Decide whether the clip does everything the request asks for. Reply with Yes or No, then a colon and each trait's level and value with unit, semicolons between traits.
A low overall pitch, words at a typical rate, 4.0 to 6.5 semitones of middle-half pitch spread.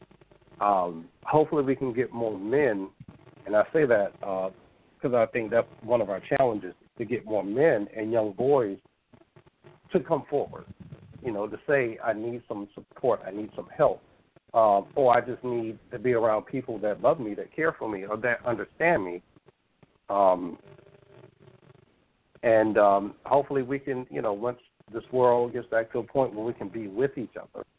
No: low, 120 Hz; average, 185 wpm; average, 3.6 semitones